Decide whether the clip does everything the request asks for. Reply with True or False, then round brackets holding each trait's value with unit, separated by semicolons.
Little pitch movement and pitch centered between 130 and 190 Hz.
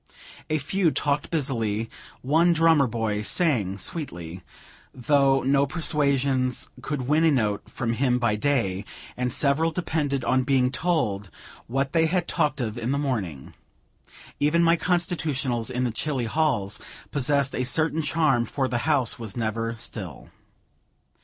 False (4.6 semitones; 135 Hz)